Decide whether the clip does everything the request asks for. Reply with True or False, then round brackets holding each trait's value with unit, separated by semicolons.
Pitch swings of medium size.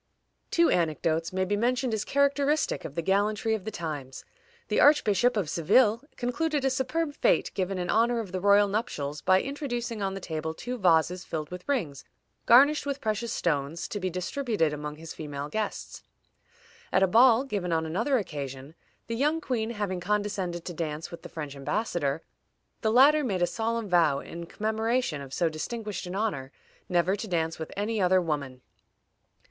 False (6.3 semitones)